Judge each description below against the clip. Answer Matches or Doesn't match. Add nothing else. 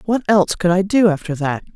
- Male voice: Doesn't match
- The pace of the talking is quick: Matches